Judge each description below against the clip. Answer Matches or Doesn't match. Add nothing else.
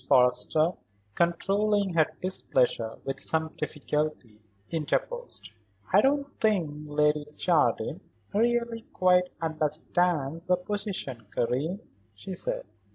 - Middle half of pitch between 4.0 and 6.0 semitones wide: Matches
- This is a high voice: Doesn't match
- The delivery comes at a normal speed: Doesn't match